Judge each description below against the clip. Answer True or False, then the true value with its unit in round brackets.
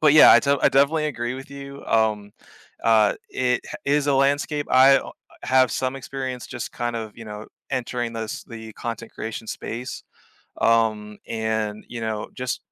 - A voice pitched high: False (120 Hz)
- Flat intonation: False (3.5 semitones)